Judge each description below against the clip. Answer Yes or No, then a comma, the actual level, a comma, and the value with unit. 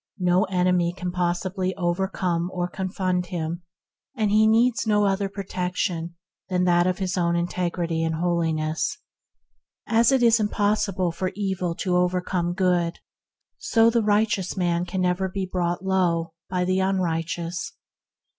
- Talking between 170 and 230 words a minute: No, average, 150 wpm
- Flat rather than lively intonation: Yes, narrow, 1.9 semitones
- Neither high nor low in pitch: Yes, medium, 180 Hz